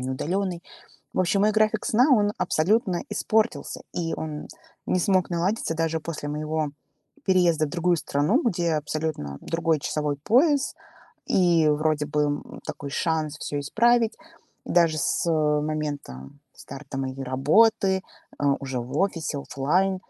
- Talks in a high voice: No, medium, 160 Hz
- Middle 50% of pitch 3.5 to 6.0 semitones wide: Yes, average, 4.3 semitones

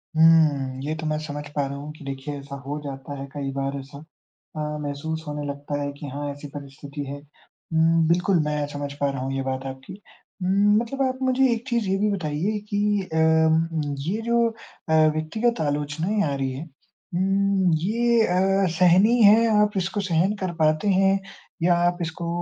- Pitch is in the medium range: Yes, medium, 160 Hz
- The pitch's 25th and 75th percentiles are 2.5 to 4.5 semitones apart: No, wide, 5.4 semitones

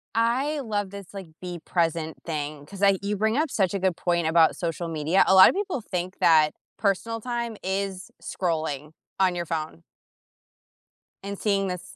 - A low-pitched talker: No, high, 190 Hz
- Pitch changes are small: No, average, 3.7 semitones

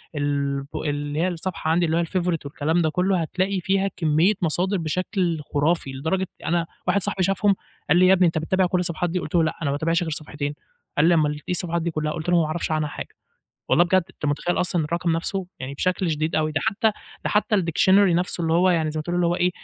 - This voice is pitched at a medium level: Yes, medium, 170 Hz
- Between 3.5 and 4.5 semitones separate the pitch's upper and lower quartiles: No, average, 2.8 semitones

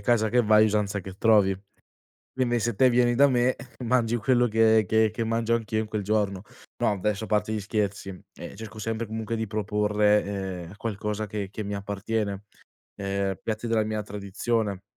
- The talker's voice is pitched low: Yes, low, 110 Hz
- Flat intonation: Yes, narrow, 1.8 semitones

